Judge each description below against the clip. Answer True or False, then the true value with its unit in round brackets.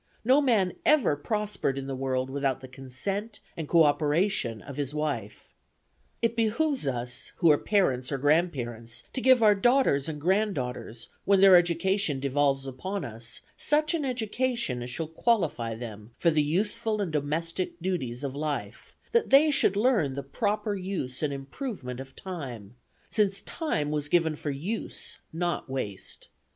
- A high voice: False (155 Hz)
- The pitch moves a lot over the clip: True (7.4 semitones)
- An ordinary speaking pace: True (155 wpm)